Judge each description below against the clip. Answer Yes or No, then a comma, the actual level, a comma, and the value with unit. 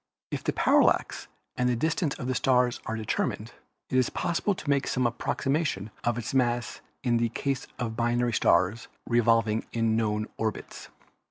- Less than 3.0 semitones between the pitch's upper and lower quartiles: Yes, narrow, 2.4 semitones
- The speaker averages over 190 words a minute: No, average, 160 wpm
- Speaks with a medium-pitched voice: No, low, 120 Hz